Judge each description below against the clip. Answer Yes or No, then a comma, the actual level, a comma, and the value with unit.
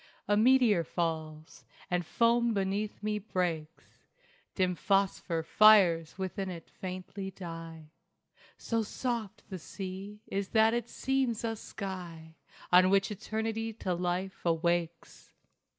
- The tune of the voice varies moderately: Yes, average, 3.9 semitones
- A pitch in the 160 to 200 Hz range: Yes, high, 190 Hz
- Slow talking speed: Yes, slow, 120 wpm